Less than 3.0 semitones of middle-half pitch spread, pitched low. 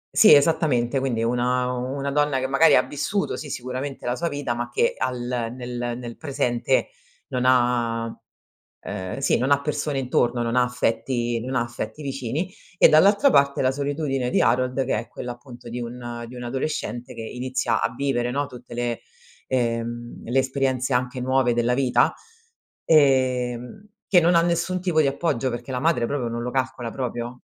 Yes: narrow, 2.5 semitones; low, 125 Hz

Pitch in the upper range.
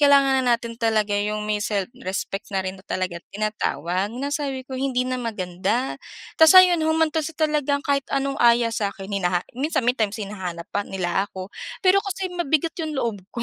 Yes: high, 235 Hz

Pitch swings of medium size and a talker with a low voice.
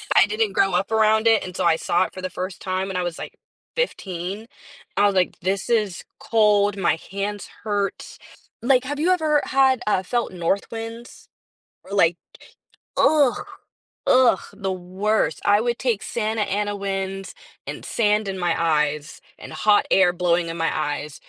No: average, 3.4 semitones; high, 200 Hz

